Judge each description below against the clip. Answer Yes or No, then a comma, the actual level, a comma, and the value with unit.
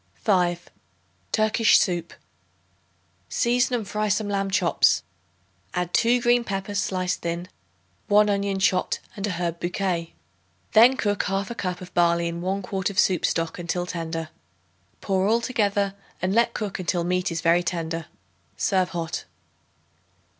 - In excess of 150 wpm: No, average, 145 wpm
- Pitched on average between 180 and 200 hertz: Yes, high, 190 Hz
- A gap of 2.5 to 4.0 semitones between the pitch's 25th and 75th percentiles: Yes, average, 2.9 semitones